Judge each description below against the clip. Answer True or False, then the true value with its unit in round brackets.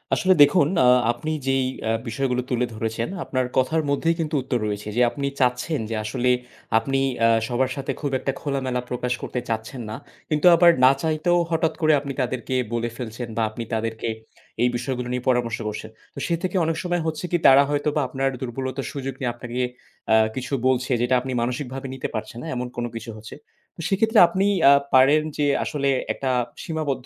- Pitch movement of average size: True (3.4 semitones)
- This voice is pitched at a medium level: False (130 Hz)